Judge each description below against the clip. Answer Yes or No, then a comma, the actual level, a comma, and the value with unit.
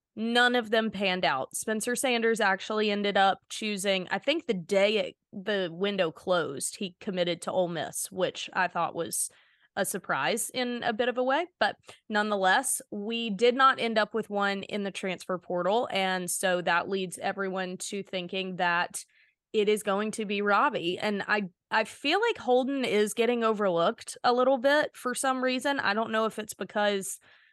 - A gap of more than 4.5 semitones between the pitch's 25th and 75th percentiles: No, average, 3.8 semitones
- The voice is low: No, high, 210 Hz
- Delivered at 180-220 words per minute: Yes, average, 185 wpm